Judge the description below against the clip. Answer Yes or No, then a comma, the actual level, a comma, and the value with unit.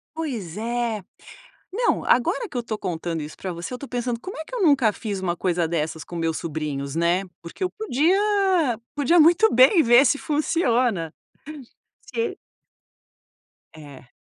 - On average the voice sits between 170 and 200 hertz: No, high, 235 Hz